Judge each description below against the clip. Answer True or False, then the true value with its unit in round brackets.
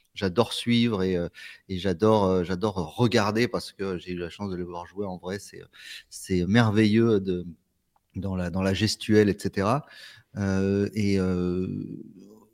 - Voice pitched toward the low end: True (95 Hz)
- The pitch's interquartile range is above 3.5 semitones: False (3.0 semitones)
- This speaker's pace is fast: False (155 wpm)